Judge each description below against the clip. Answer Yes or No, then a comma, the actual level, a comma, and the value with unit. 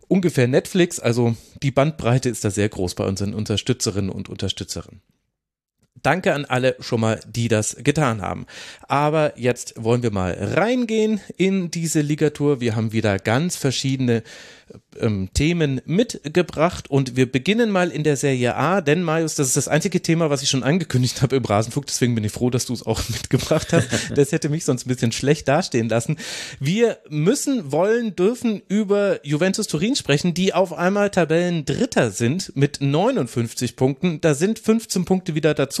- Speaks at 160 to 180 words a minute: Yes, average, 175 wpm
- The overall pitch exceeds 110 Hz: Yes, medium, 140 Hz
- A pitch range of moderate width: No, wide, 6.6 semitones